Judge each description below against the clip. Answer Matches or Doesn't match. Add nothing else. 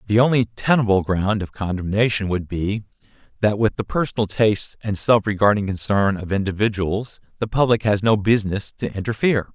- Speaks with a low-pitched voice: Matches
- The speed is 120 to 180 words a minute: Matches